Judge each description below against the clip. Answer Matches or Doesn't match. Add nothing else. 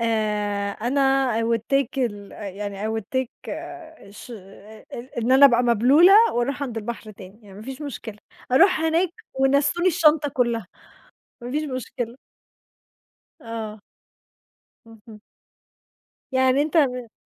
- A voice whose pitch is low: Doesn't match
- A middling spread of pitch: Matches